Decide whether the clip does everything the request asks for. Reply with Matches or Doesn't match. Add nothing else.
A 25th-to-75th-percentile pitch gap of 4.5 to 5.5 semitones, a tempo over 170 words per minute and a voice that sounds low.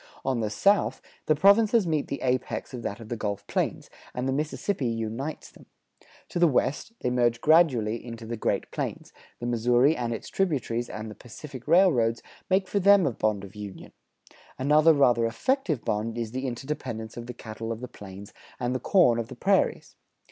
Matches